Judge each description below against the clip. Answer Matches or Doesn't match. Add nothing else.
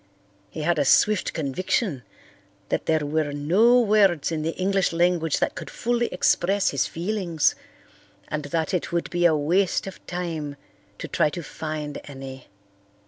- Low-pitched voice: Doesn't match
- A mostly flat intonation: Doesn't match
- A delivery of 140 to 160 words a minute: Matches